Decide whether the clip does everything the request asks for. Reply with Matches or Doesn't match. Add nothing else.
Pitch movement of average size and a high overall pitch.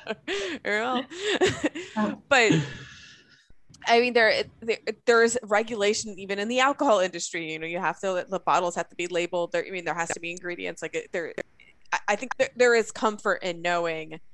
Doesn't match